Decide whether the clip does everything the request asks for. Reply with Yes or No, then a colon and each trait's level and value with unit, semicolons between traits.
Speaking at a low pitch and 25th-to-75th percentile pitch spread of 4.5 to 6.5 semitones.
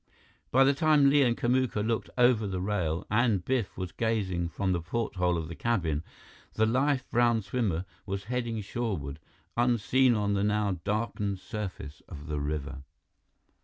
Yes: low, 105 Hz; average, 5.0 semitones